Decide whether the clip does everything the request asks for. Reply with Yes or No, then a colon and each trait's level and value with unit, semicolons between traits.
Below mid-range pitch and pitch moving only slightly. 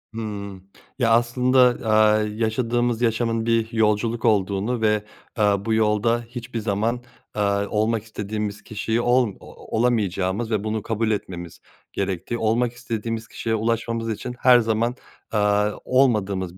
Yes: low, 110 Hz; narrow, 1.9 semitones